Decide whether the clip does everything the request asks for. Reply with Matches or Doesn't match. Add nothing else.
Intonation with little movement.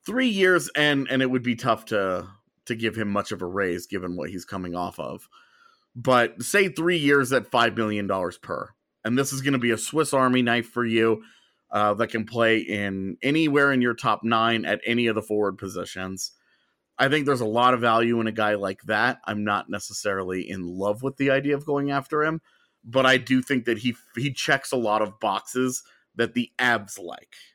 Doesn't match